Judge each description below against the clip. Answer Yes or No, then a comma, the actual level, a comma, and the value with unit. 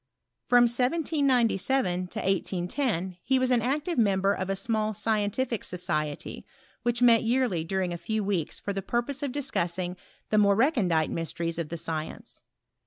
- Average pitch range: No, wide, 5.7 semitones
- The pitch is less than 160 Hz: No, high, 205 Hz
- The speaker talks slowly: No, average, 160 wpm